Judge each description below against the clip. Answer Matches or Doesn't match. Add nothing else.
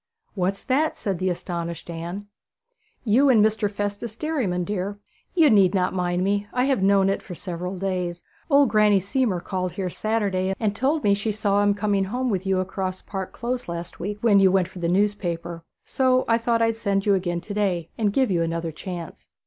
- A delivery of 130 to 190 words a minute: Doesn't match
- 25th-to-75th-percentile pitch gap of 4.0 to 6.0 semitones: Doesn't match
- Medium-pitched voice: Doesn't match